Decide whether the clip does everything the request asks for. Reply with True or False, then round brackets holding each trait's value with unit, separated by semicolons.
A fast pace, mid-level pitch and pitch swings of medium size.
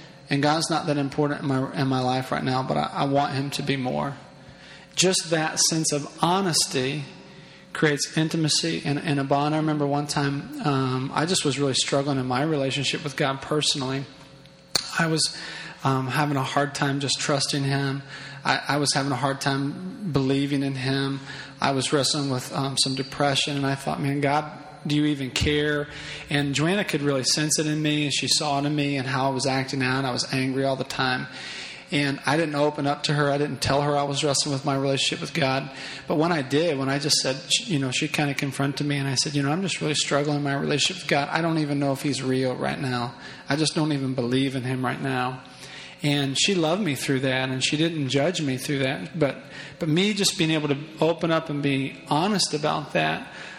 False (225 wpm; 145 Hz; 2.0 semitones)